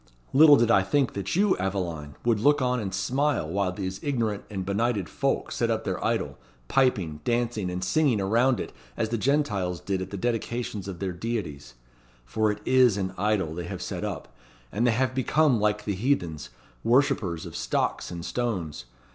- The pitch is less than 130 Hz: Yes, low, 105 Hz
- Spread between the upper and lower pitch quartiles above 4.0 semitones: Yes, average, 4.8 semitones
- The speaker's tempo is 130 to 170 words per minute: No, average, 185 wpm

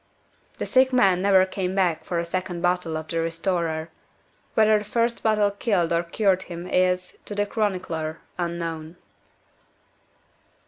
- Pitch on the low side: No, medium, 180 Hz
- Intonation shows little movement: No, average, 3.1 semitones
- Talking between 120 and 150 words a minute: Yes, average, 145 wpm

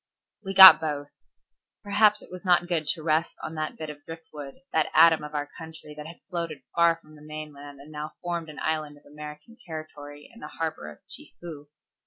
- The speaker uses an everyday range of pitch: No, narrow, 2.0 semitones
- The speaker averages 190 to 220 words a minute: Yes, fast, 205 wpm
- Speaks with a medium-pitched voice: Yes, medium, 155 Hz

